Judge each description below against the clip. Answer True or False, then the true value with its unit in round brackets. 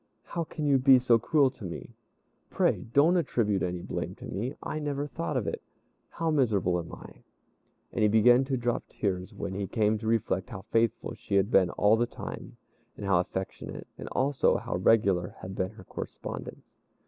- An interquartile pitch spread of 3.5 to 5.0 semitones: False (5.5 semitones)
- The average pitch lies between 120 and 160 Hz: False (110 Hz)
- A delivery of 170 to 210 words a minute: True (190 wpm)